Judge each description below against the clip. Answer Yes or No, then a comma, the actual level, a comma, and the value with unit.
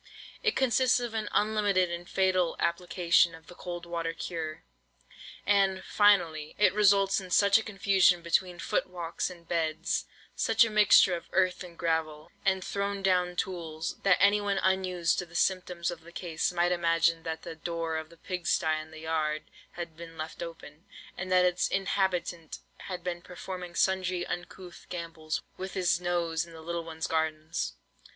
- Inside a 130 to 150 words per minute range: No, average, 165 wpm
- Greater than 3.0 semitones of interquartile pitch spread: No, narrow, 2.4 semitones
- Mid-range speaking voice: Yes, medium, 175 Hz